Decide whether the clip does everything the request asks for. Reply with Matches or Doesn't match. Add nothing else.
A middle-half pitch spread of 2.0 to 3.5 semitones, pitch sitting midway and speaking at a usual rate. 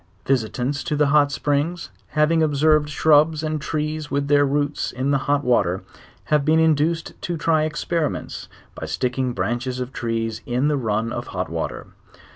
Matches